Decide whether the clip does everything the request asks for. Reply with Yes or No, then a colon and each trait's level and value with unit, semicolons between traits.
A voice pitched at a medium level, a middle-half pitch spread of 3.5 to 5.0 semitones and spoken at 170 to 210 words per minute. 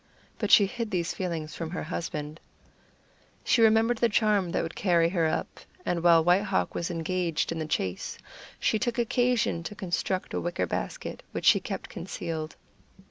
Yes: medium, 175 Hz; average, 4.1 semitones; average, 175 wpm